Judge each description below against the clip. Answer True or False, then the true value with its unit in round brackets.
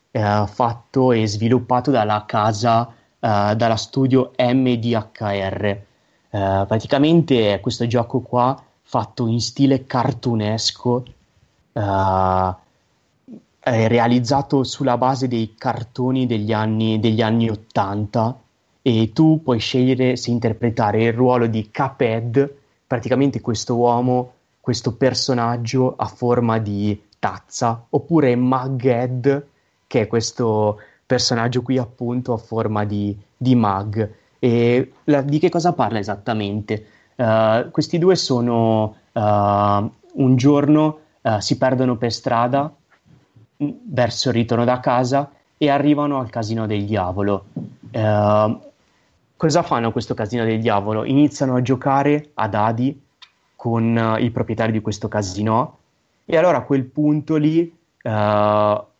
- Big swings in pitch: False (3.2 semitones)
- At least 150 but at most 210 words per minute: False (120 wpm)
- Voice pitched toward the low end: True (120 Hz)